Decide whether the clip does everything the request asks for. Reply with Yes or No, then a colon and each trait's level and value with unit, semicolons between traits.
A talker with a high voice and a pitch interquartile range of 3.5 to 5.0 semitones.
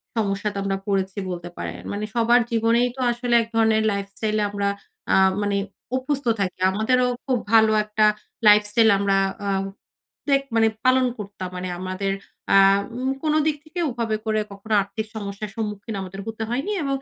No: high, 215 Hz; average, 3.1 semitones